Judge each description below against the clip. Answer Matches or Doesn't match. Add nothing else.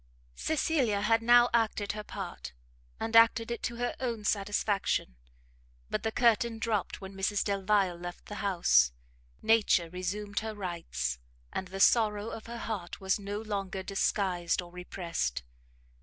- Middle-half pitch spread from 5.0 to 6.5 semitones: Doesn't match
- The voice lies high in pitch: Matches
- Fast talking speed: Doesn't match